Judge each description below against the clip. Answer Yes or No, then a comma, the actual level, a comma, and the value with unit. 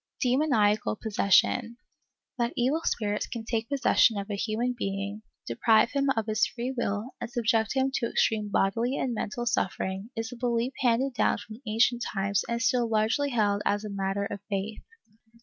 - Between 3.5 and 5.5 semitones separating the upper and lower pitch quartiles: No, average, 2.8 semitones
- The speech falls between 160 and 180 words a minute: Yes, average, 175 wpm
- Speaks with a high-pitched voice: Yes, high, 225 Hz